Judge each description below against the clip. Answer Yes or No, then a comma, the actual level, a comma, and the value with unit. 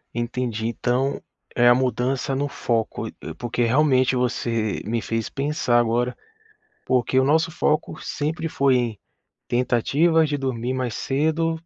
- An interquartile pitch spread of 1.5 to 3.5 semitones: Yes, average, 3.2 semitones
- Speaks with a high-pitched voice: No, low, 130 Hz